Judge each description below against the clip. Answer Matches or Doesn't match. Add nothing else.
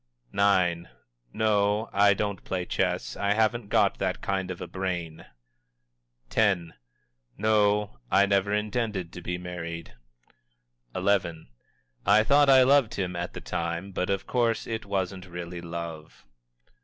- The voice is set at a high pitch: Doesn't match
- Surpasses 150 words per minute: Doesn't match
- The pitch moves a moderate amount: Matches